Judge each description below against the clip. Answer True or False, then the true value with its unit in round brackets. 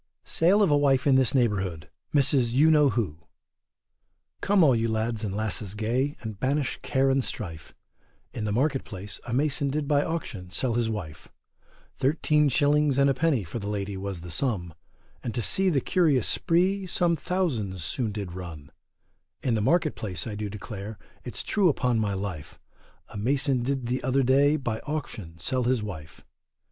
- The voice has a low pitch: True (120 Hz)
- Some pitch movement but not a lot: False (5.8 semitones)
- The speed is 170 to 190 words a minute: True (180 wpm)